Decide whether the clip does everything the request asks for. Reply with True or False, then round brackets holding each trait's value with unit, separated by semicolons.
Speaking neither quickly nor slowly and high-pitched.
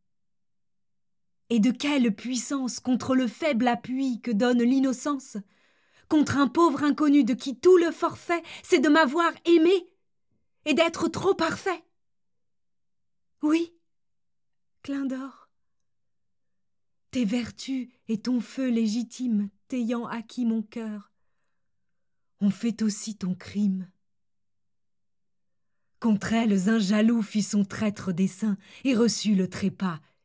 False (115 wpm; 240 Hz)